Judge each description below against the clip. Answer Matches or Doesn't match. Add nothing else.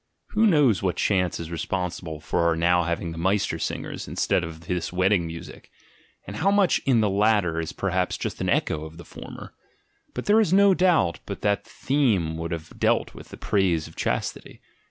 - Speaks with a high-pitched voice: Doesn't match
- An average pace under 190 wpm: Doesn't match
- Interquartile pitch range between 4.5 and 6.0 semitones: Matches